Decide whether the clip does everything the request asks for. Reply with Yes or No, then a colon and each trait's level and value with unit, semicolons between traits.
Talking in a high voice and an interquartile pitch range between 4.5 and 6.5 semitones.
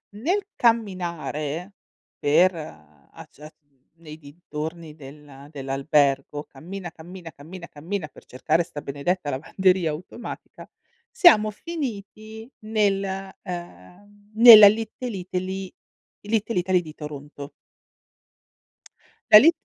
No: medium, 175 Hz; average, 5.3 semitones